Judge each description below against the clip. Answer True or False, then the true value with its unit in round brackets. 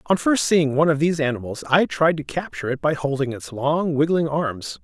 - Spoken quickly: True (225 wpm)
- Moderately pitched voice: True (150 Hz)